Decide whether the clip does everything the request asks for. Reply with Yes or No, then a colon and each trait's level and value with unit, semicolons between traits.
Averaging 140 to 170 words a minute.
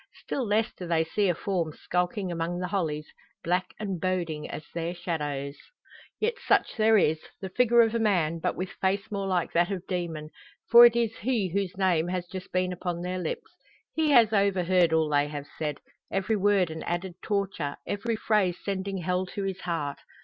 No: average, 195 wpm